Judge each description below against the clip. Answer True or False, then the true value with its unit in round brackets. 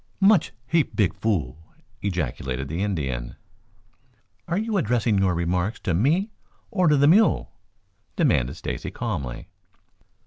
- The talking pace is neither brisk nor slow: False (125 wpm)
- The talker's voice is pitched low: True (95 Hz)